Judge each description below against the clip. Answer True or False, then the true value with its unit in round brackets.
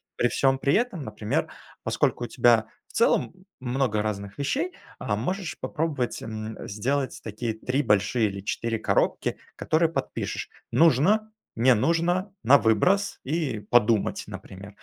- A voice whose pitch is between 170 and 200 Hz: False (125 Hz)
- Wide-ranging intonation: True (6.8 semitones)